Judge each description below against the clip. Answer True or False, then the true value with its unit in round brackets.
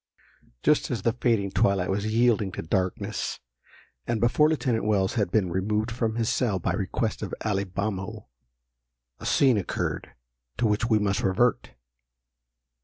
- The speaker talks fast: False (150 wpm)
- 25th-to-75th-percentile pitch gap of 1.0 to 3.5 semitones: True (3.2 semitones)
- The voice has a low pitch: True (110 Hz)